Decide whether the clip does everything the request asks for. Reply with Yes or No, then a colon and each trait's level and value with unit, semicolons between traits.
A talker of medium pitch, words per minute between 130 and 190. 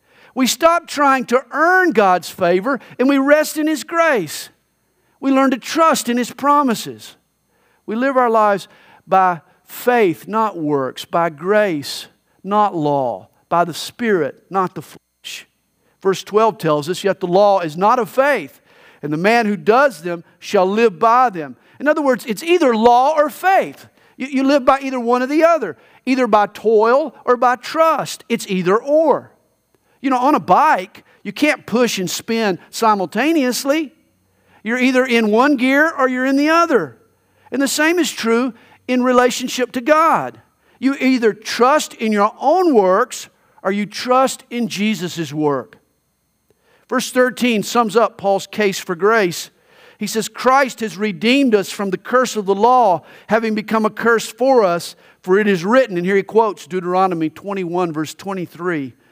No: high, 230 Hz; average, 165 wpm